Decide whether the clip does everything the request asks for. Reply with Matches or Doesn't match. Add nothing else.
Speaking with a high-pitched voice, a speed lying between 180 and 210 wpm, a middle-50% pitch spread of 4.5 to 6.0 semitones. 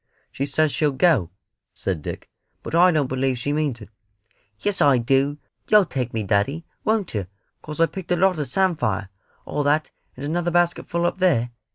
Doesn't match